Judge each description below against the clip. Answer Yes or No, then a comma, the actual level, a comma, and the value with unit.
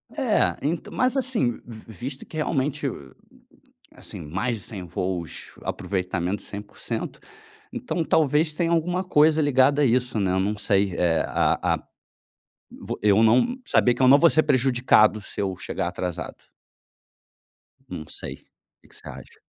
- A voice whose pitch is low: Yes, low, 125 Hz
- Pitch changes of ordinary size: No, wide, 7.4 semitones